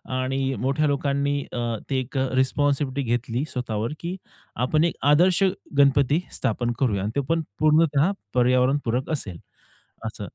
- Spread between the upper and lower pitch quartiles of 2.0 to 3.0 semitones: Yes, average, 2.7 semitones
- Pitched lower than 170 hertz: Yes, low, 135 Hz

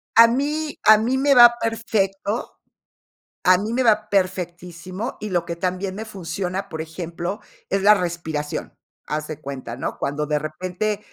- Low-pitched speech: No, high, 190 Hz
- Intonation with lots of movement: No, average, 4.2 semitones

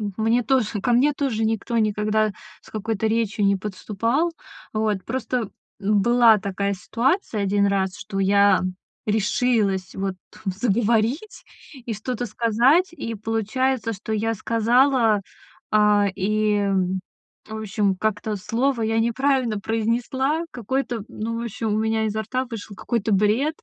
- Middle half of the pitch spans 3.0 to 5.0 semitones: No, narrow, 2.6 semitones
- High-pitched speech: Yes, high, 220 Hz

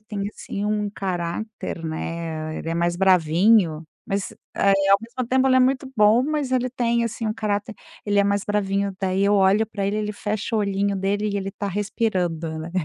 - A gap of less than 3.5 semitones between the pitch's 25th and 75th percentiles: Yes, narrow, 2.5 semitones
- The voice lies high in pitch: Yes, high, 200 Hz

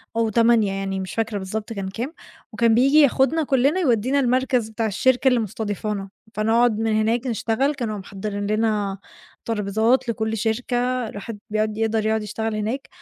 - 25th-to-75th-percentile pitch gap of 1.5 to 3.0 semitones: Yes, narrow, 2.6 semitones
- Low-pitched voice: No, high, 225 Hz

